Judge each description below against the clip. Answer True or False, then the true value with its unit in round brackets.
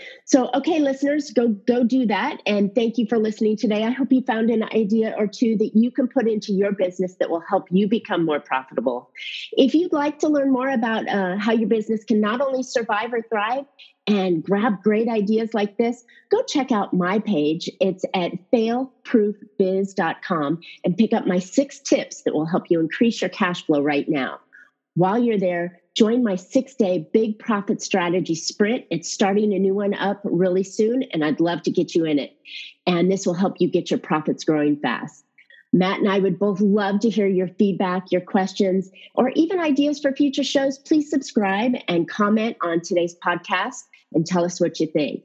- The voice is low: False (210 Hz)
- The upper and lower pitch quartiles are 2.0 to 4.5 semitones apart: False (5.1 semitones)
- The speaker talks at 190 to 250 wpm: True (200 wpm)